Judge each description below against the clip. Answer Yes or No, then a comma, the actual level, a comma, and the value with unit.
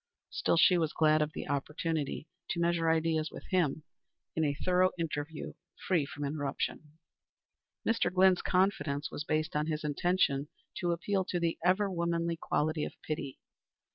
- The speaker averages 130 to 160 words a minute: Yes, average, 155 wpm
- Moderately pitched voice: Yes, medium, 160 Hz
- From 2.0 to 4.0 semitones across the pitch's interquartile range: Yes, average, 2.7 semitones